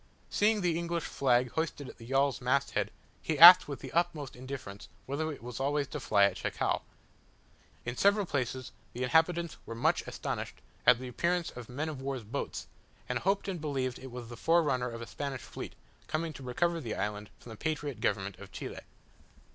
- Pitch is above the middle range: No, medium, 140 Hz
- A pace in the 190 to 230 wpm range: Yes, average, 195 wpm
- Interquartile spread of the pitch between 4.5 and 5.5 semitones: Yes, average, 4.9 semitones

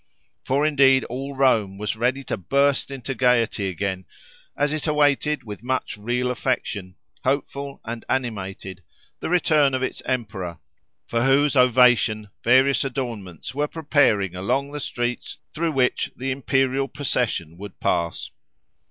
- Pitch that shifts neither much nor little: Yes, average, 4.4 semitones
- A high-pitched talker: No, low, 125 Hz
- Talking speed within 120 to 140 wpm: Yes, slow, 135 wpm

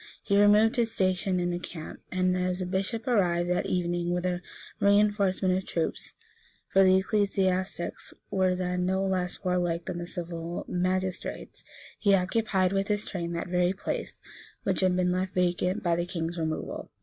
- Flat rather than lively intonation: Yes, narrow, 1.5 semitones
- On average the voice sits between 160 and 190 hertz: Yes, medium, 185 Hz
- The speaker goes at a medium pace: Yes, average, 170 wpm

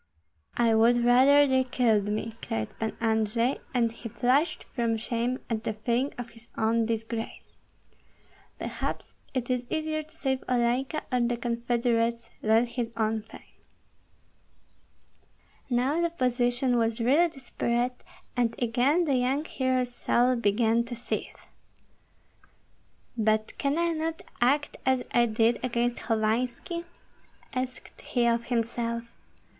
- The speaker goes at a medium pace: No, slow, 130 wpm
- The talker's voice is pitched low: No, high, 240 Hz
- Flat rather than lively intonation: Yes, narrow, 2.0 semitones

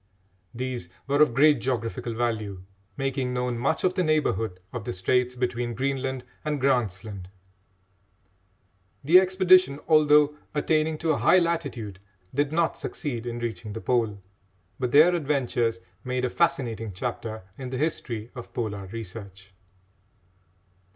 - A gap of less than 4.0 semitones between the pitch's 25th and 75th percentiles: No, average, 4.6 semitones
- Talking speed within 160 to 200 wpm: No, slow, 135 wpm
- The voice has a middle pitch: No, low, 125 Hz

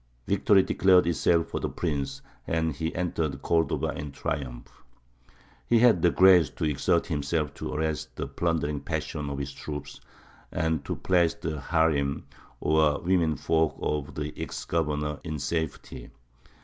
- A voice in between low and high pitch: No, very low, 80 Hz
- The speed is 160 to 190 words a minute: No, average, 150 wpm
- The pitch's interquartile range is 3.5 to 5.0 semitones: No, narrow, 2.4 semitones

